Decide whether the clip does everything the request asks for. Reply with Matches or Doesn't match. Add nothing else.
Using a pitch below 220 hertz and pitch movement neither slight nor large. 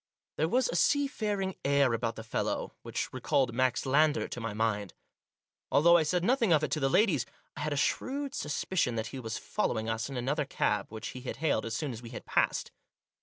Doesn't match